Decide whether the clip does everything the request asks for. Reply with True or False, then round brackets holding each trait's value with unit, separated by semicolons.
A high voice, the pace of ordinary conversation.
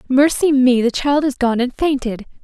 True (260 Hz; 195 wpm)